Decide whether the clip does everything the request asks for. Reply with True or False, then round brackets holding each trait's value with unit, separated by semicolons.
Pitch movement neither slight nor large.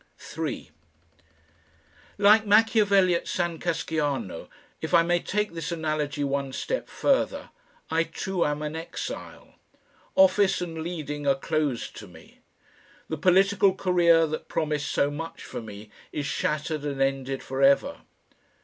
True (4.1 semitones)